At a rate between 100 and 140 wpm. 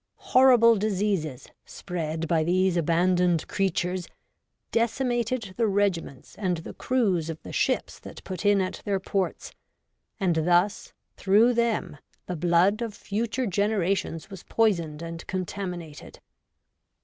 Yes: slow, 135 wpm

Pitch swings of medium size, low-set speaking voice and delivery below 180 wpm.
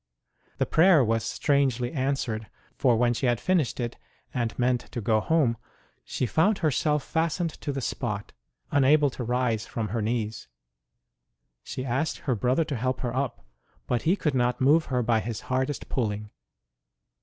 Yes: average, 3.6 semitones; low, 125 Hz; average, 165 wpm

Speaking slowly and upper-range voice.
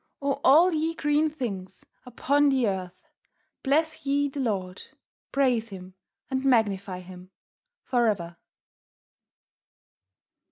Yes: slow, 110 wpm; very high, 250 Hz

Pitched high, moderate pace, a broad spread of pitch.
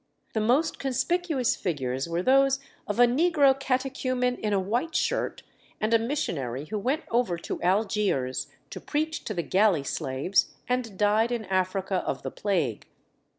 Yes: high, 220 Hz; average, 155 wpm; wide, 6.1 semitones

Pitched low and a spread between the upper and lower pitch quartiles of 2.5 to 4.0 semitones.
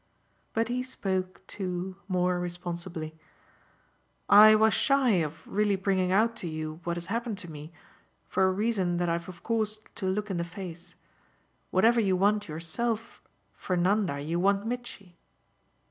No: medium, 185 Hz; average, 3.6 semitones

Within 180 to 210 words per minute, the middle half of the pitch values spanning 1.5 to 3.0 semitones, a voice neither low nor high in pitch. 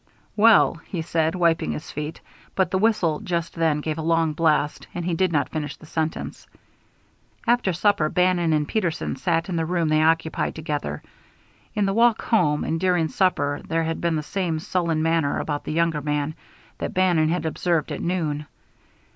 Yes: average, 185 wpm; narrow, 2.6 semitones; medium, 165 Hz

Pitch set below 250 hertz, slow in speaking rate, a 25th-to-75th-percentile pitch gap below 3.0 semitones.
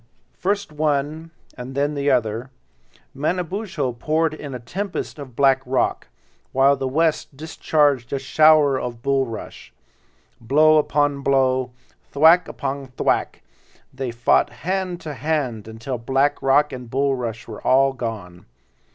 No: medium, 140 Hz; slow, 125 wpm; average, 3.4 semitones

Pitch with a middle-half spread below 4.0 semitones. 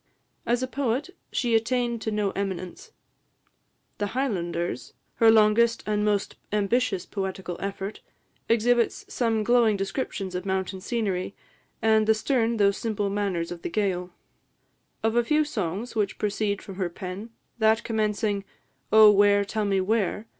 Yes: average, 2.7 semitones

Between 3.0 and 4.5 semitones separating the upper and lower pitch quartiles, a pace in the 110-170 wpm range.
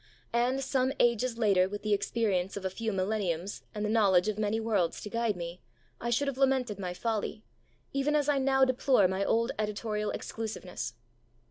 No: average, 3.9 semitones; average, 185 wpm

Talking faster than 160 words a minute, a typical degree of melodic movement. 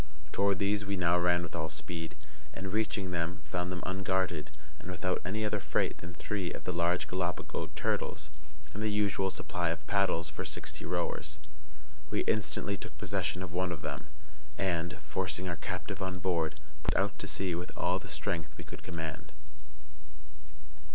No: average, 170 wpm; narrow, 2.2 semitones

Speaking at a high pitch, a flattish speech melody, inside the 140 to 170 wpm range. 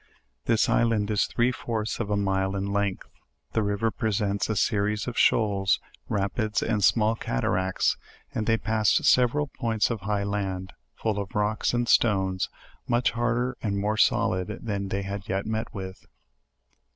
No: low, 105 Hz; narrow, 2.3 semitones; average, 165 wpm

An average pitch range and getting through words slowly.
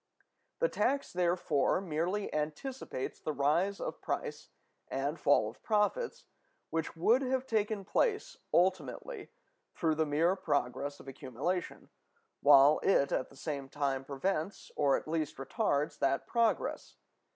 No: wide, 6.0 semitones; slow, 130 wpm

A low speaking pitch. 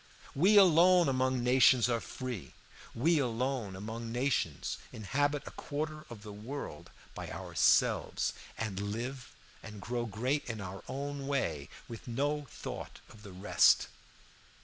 Yes: low, 125 Hz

